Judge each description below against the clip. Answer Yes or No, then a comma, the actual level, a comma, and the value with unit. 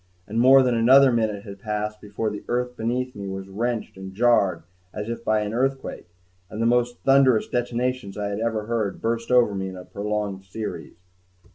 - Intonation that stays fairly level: No, average, 3.1 semitones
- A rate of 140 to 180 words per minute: No, average, 190 wpm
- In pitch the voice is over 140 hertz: No, low, 110 Hz